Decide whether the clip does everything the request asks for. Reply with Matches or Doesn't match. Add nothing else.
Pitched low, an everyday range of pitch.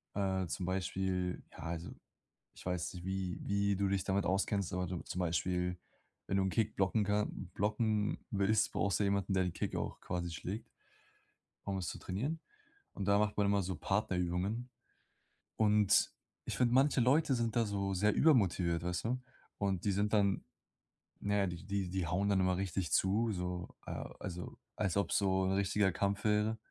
Doesn't match